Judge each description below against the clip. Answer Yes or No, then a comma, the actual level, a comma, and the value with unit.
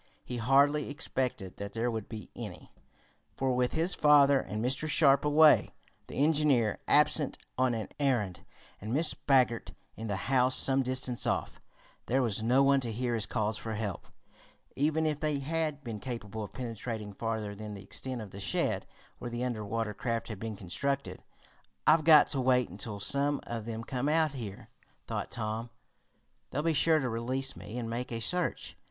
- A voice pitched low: Yes, low, 125 Hz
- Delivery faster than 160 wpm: Yes, average, 180 wpm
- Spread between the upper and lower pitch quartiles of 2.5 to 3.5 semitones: No, average, 4.0 semitones